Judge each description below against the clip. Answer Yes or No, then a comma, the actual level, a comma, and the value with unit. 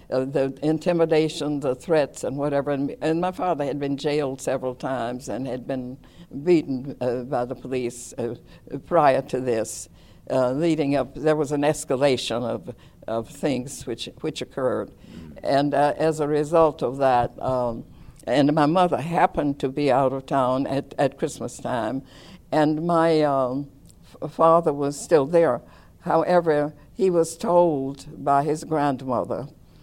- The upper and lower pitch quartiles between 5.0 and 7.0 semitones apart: No, average, 3.3 semitones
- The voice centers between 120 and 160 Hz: Yes, medium, 140 Hz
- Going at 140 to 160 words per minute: Yes, average, 155 wpm